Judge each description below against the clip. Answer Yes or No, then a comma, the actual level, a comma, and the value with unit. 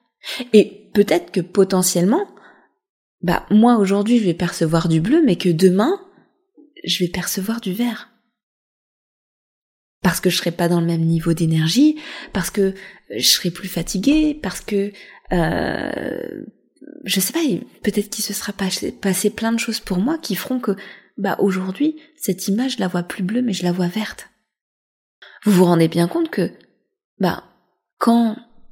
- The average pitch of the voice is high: Yes, high, 205 Hz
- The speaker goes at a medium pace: Yes, average, 160 wpm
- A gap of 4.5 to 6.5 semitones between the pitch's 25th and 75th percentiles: Yes, average, 4.9 semitones